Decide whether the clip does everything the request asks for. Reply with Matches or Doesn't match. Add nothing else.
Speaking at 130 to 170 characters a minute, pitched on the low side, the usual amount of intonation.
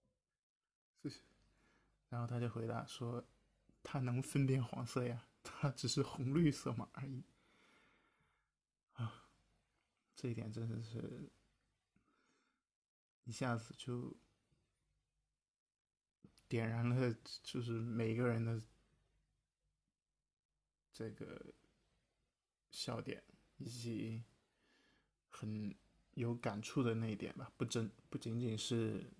Doesn't match